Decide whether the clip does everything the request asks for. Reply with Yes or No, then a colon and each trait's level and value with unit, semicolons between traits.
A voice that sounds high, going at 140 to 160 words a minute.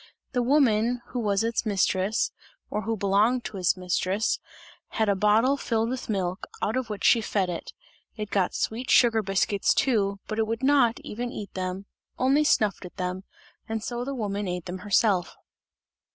No: high, 215 Hz; average, 180 wpm